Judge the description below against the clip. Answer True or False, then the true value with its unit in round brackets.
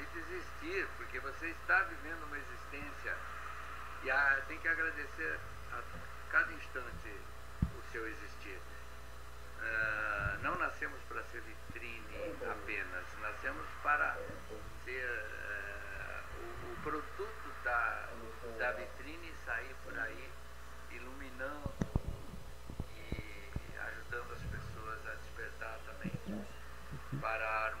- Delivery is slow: True (100 wpm)